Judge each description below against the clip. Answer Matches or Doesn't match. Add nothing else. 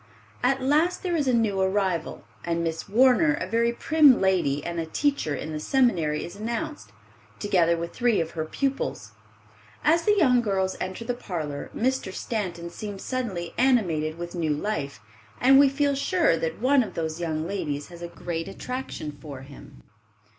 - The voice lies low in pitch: Doesn't match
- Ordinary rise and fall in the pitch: Doesn't match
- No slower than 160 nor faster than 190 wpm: Matches